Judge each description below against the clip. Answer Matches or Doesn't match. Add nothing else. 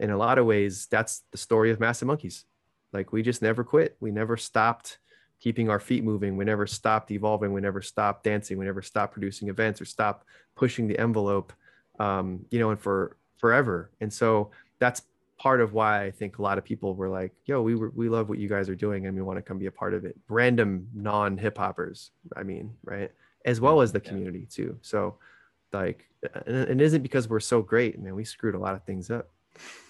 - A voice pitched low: Matches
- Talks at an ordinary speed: Doesn't match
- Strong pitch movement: Doesn't match